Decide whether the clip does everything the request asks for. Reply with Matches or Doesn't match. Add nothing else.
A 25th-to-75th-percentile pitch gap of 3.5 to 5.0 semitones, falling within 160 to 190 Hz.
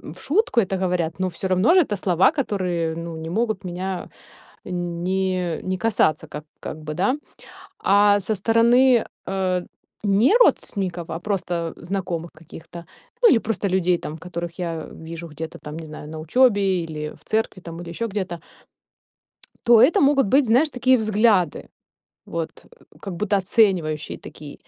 Matches